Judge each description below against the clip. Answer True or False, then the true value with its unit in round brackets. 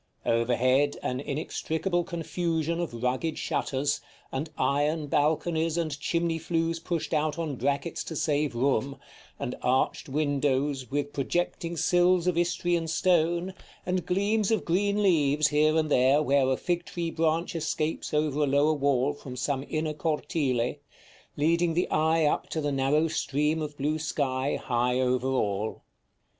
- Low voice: False (150 Hz)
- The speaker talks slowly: False (150 wpm)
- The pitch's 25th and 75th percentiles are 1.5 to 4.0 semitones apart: True (3.1 semitones)